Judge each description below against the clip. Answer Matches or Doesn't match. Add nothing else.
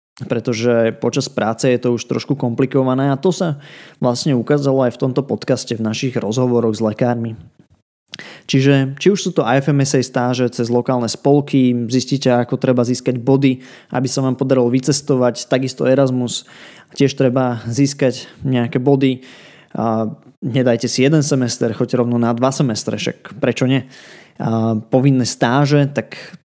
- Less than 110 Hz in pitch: Doesn't match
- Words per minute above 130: Matches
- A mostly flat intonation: Matches